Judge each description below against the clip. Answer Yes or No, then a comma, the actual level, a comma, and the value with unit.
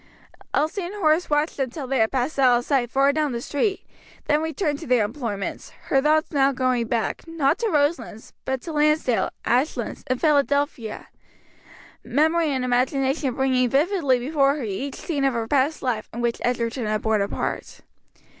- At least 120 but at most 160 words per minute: No, average, 180 wpm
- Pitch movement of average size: Yes, average, 3.7 semitones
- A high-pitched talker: Yes, very high, 270 Hz